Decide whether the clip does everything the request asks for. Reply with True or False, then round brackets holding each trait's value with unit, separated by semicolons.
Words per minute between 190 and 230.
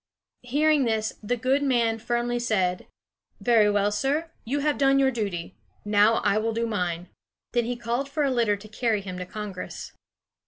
False (180 wpm)